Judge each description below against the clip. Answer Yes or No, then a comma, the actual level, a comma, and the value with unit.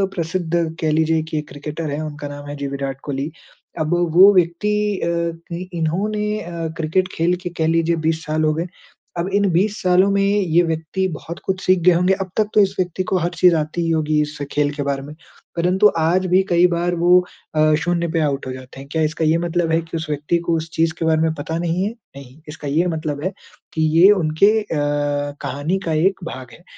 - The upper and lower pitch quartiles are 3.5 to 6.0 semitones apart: No, average, 2.7 semitones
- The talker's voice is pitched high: No, medium, 165 Hz